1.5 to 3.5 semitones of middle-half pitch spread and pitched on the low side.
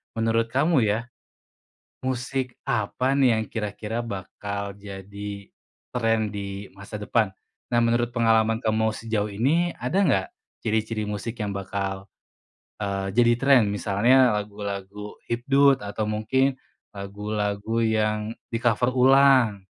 Yes: average, 2.9 semitones; low, 110 Hz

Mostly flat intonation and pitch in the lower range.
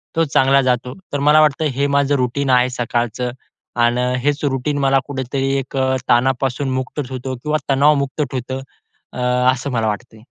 Yes: narrow, 2.1 semitones; low, 130 Hz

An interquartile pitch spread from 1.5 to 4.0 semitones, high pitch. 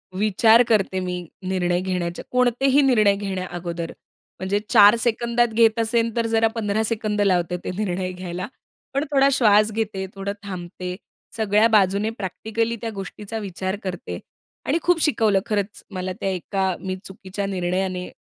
Yes: average, 3.4 semitones; high, 200 Hz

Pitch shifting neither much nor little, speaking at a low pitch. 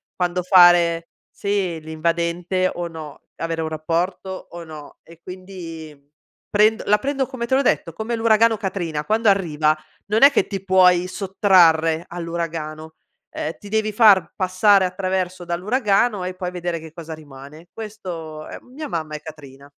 No: average, 3.6 semitones; medium, 180 Hz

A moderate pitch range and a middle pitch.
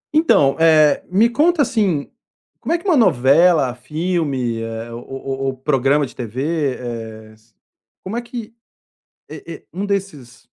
No: wide, 7.8 semitones; medium, 145 Hz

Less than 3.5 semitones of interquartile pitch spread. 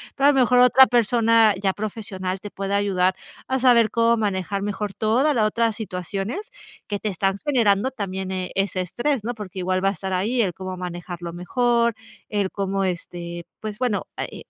No: average, 3.8 semitones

